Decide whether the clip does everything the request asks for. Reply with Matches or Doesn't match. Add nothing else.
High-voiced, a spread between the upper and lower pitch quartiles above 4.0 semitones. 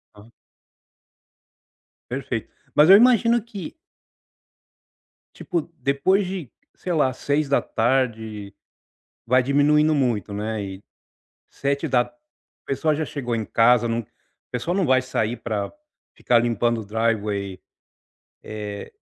Doesn't match